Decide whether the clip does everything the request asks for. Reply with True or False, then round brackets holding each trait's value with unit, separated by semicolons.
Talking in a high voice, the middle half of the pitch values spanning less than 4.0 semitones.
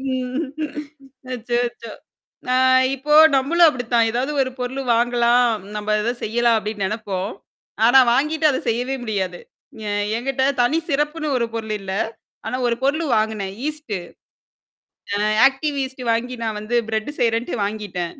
True (240 Hz; 3.6 semitones)